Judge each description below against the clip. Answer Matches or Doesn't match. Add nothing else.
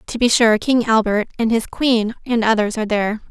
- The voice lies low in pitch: Doesn't match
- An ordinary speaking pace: Doesn't match